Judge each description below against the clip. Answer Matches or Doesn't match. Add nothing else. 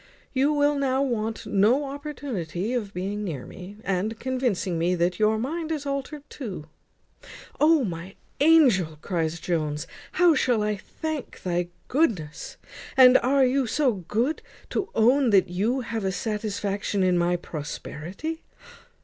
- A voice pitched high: Matches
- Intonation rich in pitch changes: Matches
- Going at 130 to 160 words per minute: Matches